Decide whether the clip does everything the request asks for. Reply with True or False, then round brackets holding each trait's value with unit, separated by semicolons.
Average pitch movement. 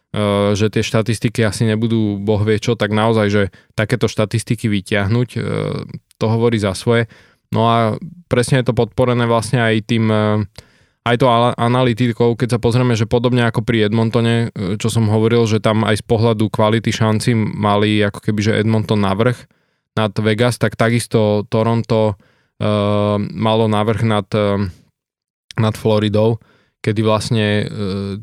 False (1.8 semitones)